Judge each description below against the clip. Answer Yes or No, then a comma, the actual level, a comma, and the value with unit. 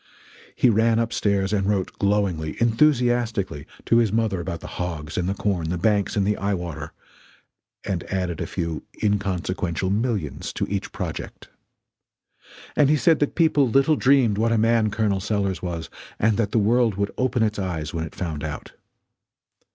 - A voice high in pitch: No, low, 100 Hz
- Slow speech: No, average, 175 wpm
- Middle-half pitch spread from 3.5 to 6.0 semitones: Yes, average, 4.2 semitones